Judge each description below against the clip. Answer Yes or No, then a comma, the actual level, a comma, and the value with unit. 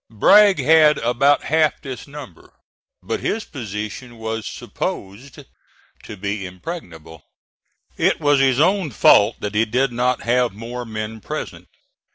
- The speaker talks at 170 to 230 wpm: No, slow, 135 wpm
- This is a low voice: Yes, low, 120 Hz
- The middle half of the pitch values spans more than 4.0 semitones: Yes, average, 5.1 semitones